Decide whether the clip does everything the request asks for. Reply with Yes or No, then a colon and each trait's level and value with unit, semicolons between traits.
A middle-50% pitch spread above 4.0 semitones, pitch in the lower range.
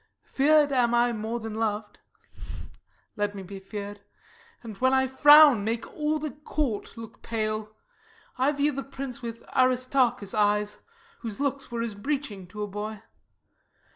No: average, 4.5 semitones; high, 230 Hz